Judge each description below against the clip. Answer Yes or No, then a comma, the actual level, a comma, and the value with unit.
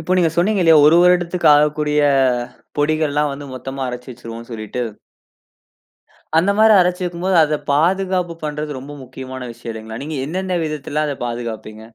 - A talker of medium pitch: Yes, medium, 150 Hz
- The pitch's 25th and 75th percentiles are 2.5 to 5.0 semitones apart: No, wide, 5.4 semitones